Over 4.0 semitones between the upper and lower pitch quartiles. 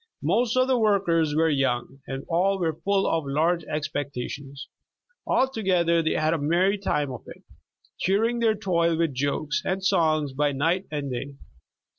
Yes: average, 5.1 semitones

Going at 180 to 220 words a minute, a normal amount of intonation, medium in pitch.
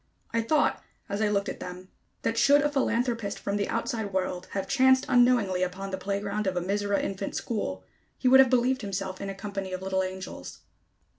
No: average, 200 wpm; average, 3.8 semitones; high, 200 Hz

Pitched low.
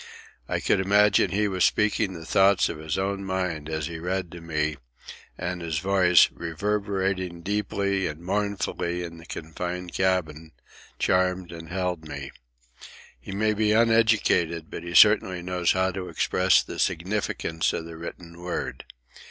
Yes: very low, 90 Hz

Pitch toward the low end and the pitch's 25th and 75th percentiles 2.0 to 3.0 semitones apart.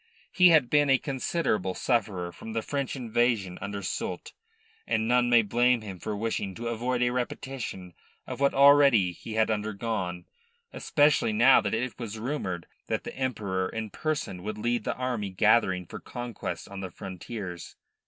No: low, 115 Hz; average, 4.2 semitones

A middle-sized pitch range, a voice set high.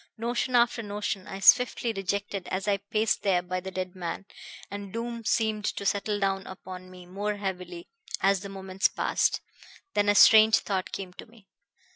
No: narrow, 2.2 semitones; high, 200 Hz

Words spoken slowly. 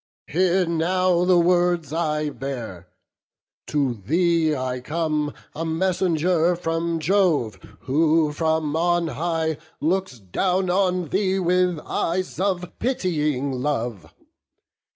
Yes: slow, 110 wpm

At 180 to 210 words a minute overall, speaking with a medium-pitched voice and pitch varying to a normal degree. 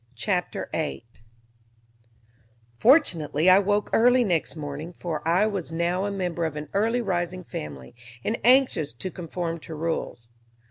No: average, 140 wpm; medium, 175 Hz; average, 4.3 semitones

